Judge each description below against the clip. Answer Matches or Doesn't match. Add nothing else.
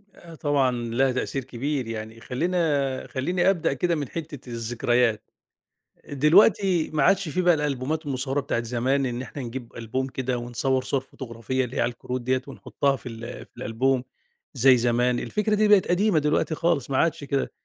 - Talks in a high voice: Doesn't match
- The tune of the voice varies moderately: Matches